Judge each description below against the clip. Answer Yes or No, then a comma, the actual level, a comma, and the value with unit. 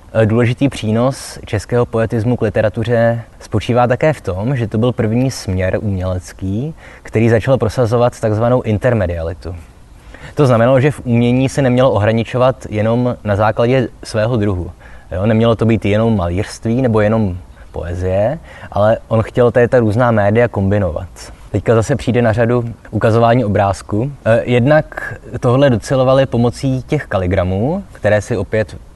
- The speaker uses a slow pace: No, average, 135 wpm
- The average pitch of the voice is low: Yes, low, 115 Hz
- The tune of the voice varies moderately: Yes, average, 3.0 semitones